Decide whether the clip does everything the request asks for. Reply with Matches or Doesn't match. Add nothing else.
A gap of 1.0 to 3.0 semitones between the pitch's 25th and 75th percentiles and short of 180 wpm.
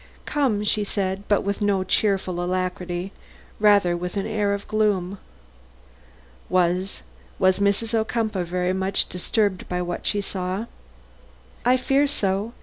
Matches